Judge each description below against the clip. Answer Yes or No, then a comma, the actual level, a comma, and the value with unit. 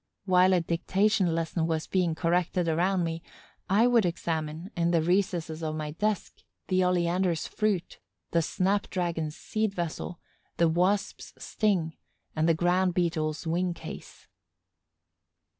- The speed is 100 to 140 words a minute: Yes, slow, 135 wpm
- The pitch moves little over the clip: Yes, narrow, 2.3 semitones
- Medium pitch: Yes, medium, 175 Hz